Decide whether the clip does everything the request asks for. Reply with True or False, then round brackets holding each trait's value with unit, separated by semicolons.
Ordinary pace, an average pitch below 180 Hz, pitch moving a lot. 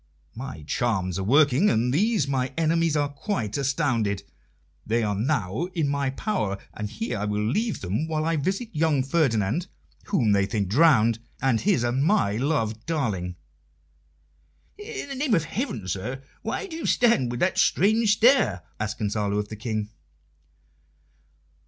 True (160 wpm; 135 Hz; 7.8 semitones)